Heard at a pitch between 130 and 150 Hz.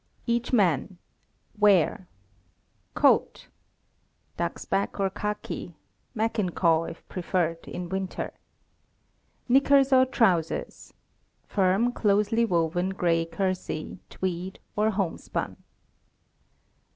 No: high, 190 Hz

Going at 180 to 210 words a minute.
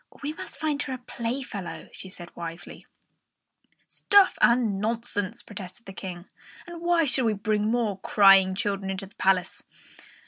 No: average, 150 wpm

